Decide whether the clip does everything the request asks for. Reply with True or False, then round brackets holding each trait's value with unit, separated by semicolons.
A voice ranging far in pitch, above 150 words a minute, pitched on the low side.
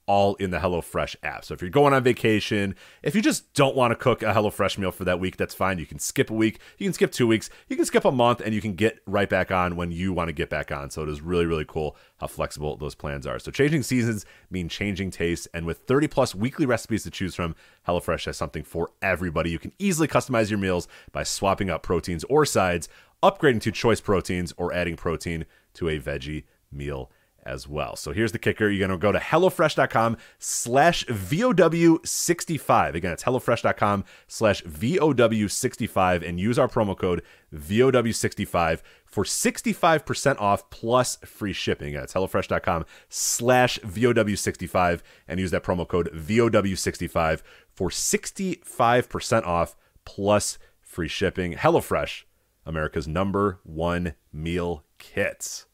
True (5.9 semitones; 175 wpm; 100 Hz)